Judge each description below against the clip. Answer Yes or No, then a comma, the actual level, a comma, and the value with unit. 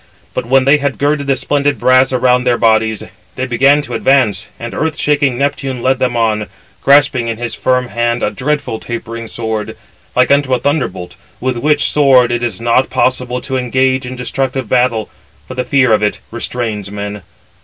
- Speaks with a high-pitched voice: No, low, 125 Hz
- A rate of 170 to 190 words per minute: Yes, average, 185 wpm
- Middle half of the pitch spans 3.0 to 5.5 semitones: No, narrow, 2.5 semitones